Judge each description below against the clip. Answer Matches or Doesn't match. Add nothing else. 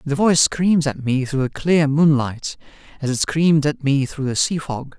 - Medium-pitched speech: Matches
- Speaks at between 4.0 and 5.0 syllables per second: Matches